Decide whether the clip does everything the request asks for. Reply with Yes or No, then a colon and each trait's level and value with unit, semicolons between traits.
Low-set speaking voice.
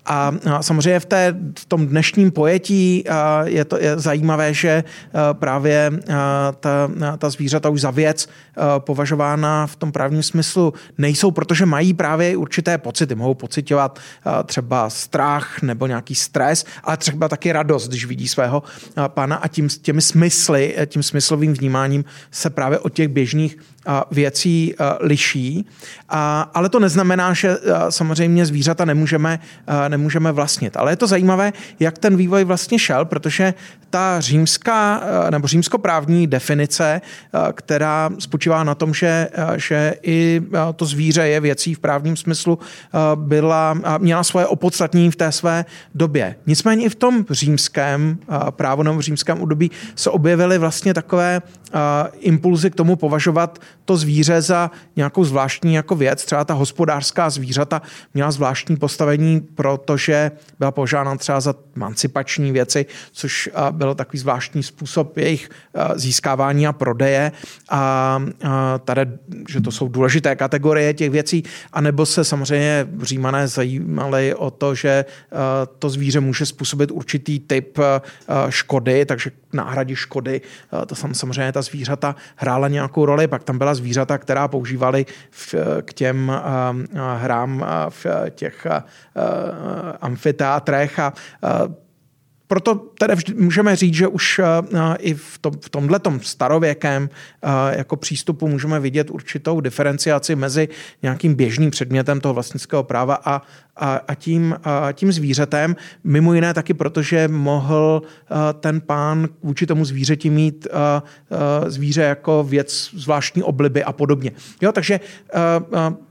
No: medium, 150 Hz